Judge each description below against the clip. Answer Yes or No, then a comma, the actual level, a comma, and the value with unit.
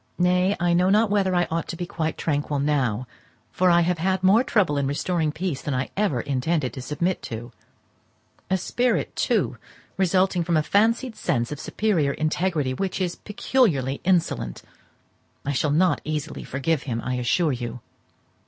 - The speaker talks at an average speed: Yes, average, 165 wpm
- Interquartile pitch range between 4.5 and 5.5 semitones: Yes, average, 5.0 semitones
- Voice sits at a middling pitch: Yes, medium, 165 Hz